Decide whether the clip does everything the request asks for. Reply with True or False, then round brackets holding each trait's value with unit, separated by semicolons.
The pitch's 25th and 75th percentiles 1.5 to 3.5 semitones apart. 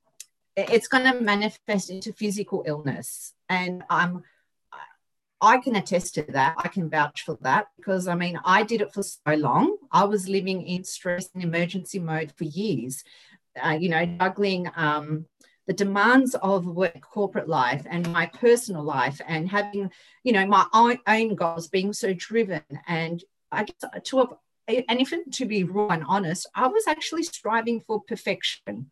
False (4.0 semitones)